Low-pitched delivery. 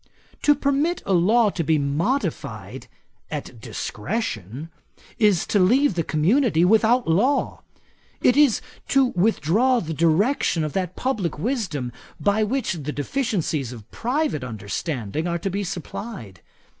No: high, 190 Hz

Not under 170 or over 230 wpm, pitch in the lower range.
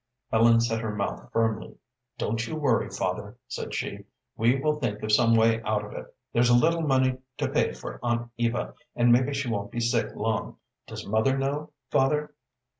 Yes: average, 190 wpm; low, 120 Hz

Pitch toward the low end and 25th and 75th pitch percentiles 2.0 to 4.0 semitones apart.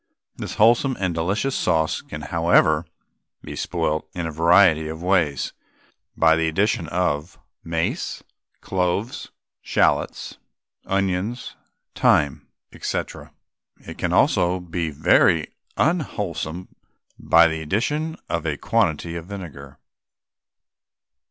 Yes: very low, 85 Hz; average, 3.6 semitones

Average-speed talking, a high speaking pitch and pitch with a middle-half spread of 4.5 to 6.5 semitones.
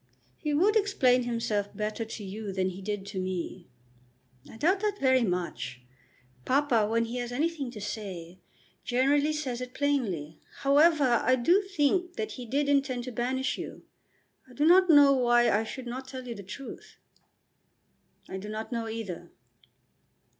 Yes: average, 165 wpm; high, 245 Hz; average, 5.2 semitones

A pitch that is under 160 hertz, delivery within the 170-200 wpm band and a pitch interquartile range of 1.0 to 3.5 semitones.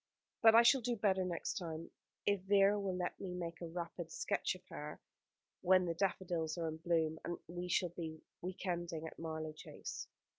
No: medium, 175 Hz; average, 190 wpm; narrow, 2.5 semitones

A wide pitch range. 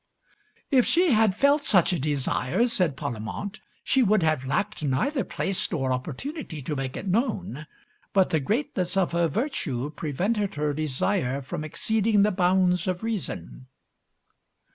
Yes: wide, 6.7 semitones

